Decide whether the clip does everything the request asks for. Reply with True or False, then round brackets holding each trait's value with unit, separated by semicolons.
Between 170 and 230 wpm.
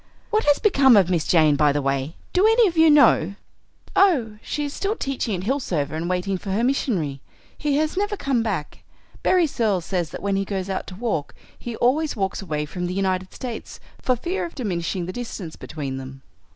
True (205 wpm)